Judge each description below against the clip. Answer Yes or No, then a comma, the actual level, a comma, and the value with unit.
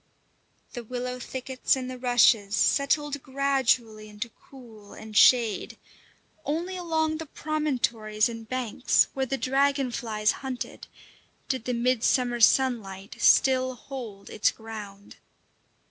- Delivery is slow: Yes, slow, 115 wpm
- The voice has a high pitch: Yes, very high, 250 Hz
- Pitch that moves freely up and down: No, average, 3.5 semitones